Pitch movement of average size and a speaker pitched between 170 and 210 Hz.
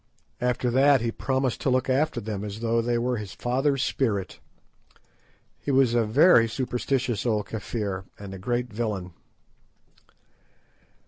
No: average, 3.4 semitones; low, 120 Hz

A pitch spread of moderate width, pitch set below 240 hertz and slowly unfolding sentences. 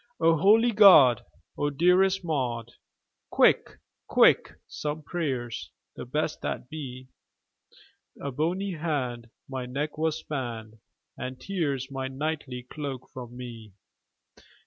Yes: average, 4.4 semitones; medium, 140 Hz; slow, 115 wpm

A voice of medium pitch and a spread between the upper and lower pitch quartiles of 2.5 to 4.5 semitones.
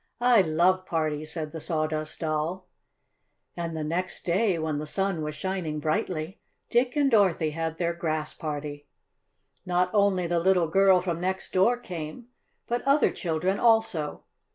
Yes: medium, 170 Hz; average, 3.5 semitones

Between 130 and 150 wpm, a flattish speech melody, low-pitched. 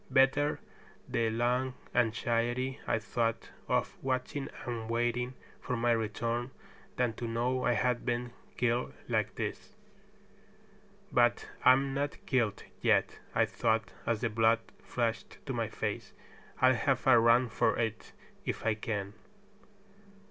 Yes: slow, 135 wpm; narrow, 1.9 semitones; low, 120 Hz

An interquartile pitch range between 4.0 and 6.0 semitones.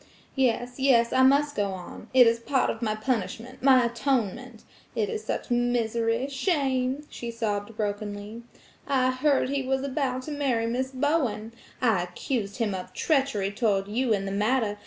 No: average, 3.6 semitones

